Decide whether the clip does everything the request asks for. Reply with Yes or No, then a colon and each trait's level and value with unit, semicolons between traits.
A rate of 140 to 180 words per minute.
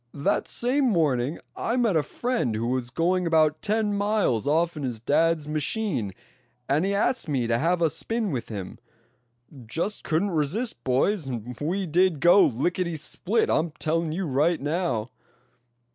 Yes: average, 160 wpm